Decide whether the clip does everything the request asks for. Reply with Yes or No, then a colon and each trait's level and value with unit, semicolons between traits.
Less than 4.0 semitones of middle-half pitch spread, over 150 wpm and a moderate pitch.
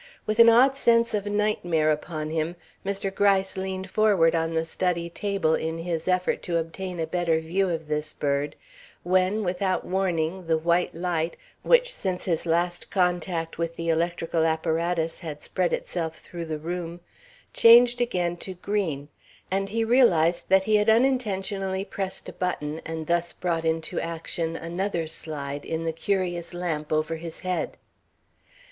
Yes: average, 2.9 semitones; average, 160 wpm; medium, 175 Hz